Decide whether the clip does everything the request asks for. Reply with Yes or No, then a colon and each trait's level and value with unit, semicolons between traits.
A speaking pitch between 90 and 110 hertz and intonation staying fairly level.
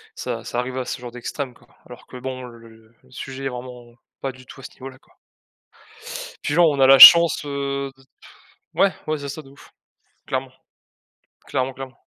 No: low, 130 Hz; narrow, 1.8 semitones